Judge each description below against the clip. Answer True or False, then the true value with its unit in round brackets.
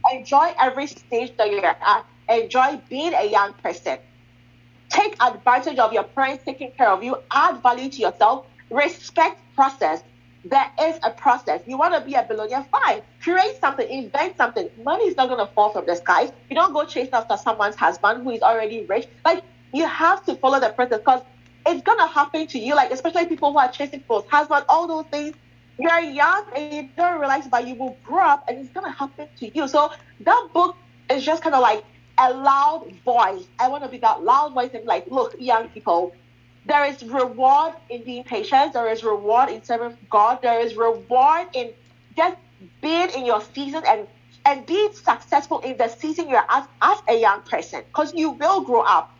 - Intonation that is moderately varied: False (5.7 semitones)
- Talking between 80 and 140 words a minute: False (205 wpm)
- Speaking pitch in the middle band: False (270 Hz)